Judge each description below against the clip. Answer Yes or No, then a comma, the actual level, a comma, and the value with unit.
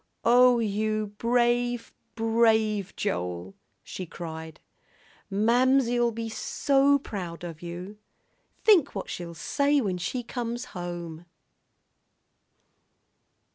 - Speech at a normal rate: No, slow, 95 wpm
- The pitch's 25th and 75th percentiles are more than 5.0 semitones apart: Yes, wide, 5.6 semitones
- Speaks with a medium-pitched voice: No, high, 220 Hz